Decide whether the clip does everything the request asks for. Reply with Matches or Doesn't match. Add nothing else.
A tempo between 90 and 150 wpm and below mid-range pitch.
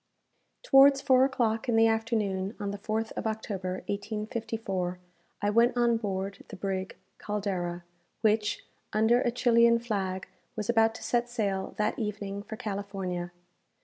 Doesn't match